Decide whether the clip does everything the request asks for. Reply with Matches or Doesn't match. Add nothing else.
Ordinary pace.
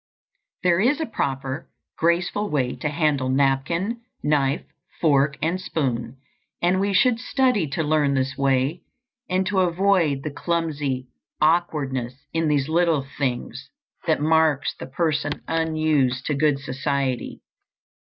Doesn't match